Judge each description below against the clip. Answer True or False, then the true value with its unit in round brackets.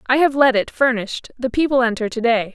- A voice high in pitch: True (245 Hz)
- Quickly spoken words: True (235 wpm)